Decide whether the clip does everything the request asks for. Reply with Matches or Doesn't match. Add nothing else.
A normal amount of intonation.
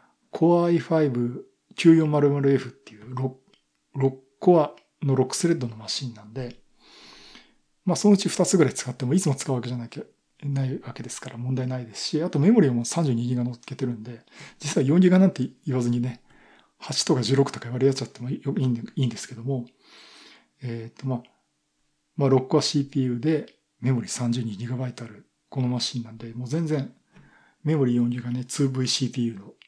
Matches